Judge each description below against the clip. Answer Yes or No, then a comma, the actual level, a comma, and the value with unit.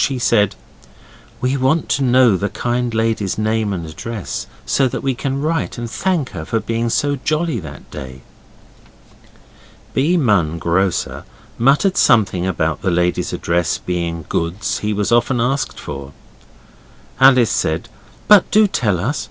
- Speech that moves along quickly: No, average, 150 wpm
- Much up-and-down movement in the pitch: Yes, wide, 7.0 semitones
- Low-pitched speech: Yes, low, 115 Hz